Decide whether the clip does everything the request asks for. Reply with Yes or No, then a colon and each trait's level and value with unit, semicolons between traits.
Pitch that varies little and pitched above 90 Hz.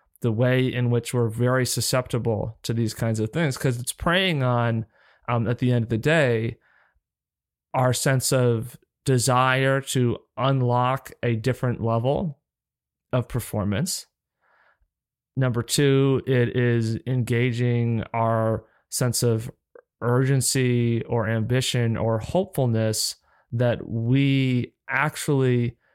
Yes: narrow, 2.1 semitones; low, 125 Hz